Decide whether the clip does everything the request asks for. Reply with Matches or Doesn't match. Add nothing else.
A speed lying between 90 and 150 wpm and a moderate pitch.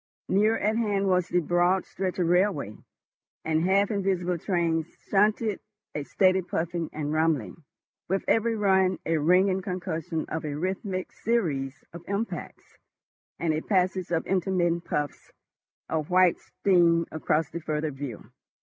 Matches